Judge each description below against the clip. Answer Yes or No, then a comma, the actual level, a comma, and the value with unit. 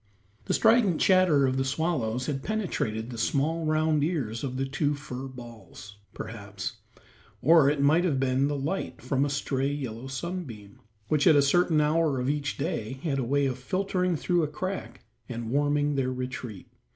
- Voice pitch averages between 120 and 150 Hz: Yes, medium, 140 Hz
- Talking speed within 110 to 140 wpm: No, average, 175 wpm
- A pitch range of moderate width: Yes, average, 3.7 semitones